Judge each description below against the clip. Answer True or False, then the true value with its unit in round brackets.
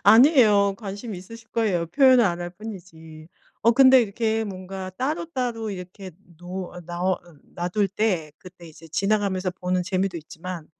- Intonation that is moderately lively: True (3.9 semitones)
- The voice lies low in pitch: False (195 Hz)